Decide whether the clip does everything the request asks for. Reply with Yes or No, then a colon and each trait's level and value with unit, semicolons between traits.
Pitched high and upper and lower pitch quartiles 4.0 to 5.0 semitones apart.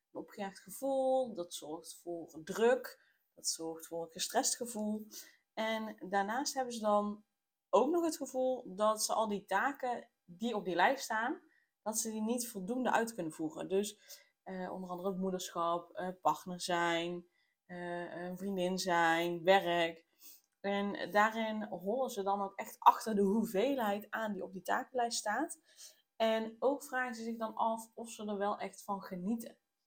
Yes: high, 210 Hz; average, 4.6 semitones